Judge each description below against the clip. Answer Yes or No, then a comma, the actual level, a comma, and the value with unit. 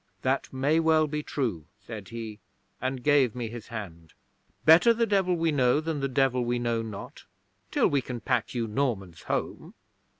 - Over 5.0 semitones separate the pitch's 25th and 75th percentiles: No, average, 4.7 semitones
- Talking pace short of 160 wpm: No, average, 175 wpm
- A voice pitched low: Yes, low, 125 Hz